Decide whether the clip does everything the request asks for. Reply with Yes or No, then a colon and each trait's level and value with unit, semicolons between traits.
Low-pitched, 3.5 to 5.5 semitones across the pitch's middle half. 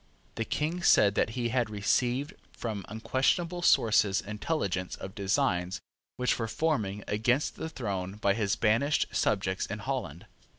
Yes: low, 110 Hz; average, 4.7 semitones